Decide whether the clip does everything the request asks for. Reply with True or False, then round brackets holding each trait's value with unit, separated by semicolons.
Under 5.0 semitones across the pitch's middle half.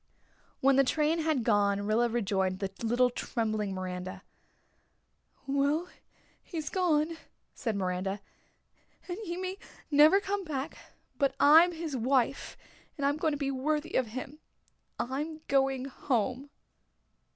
False (5.6 semitones)